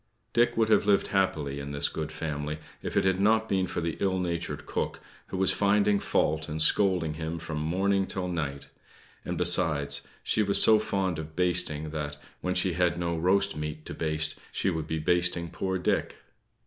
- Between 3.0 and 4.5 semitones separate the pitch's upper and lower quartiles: Yes, average, 3.6 semitones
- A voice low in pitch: Yes, very low, 85 Hz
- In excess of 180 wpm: Yes, average, 190 wpm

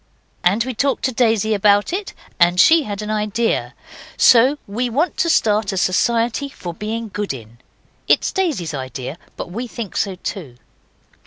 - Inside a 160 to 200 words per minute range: Yes, average, 170 wpm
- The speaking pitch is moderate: No, high, 215 Hz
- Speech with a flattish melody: No, average, 4.9 semitones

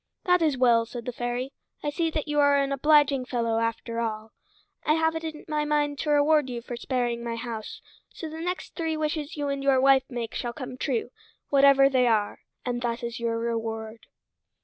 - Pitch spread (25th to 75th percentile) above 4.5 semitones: No, average, 4.1 semitones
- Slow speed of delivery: No, fast, 205 wpm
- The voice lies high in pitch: Yes, very high, 260 Hz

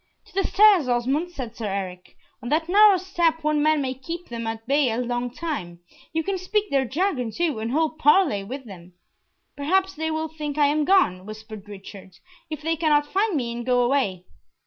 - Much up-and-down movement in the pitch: Yes, wide, 6.0 semitones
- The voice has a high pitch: Yes, very high, 285 Hz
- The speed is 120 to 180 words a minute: No, average, 200 wpm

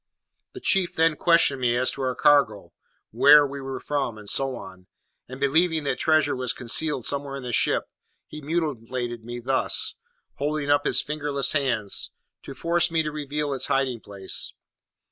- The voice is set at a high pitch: No, medium, 140 Hz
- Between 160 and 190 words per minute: Yes, average, 170 wpm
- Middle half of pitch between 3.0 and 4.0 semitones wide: Yes, average, 3.3 semitones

